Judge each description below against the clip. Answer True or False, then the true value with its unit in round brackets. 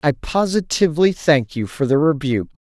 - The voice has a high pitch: False (145 Hz)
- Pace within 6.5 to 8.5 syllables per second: False (5.4 syllables/s)